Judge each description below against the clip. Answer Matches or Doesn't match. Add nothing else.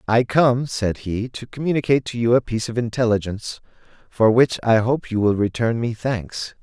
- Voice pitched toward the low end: Matches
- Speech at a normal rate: Matches